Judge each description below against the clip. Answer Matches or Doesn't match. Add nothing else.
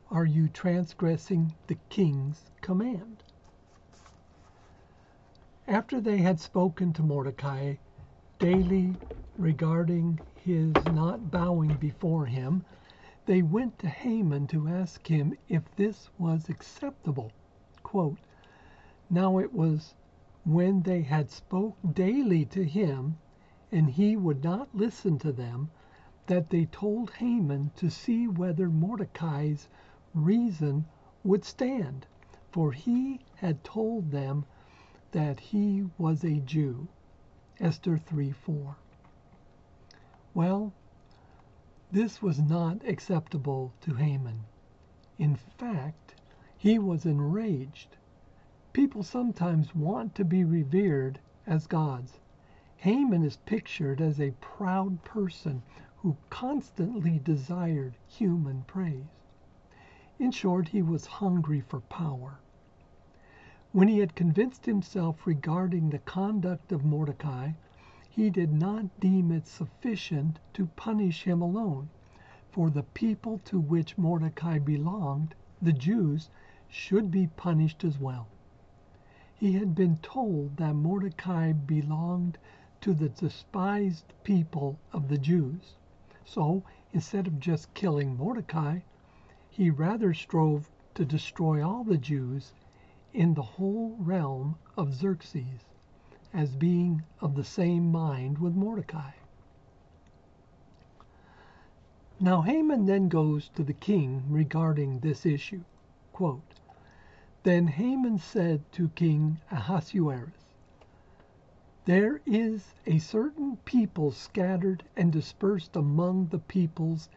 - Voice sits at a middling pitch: Matches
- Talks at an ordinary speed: Doesn't match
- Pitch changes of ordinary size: Matches